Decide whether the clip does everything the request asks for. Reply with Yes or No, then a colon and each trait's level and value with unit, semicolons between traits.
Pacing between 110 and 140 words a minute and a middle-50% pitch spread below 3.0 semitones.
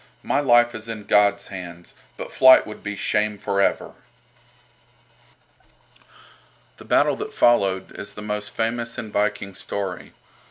Yes: slow, 135 wpm; narrow, 2.4 semitones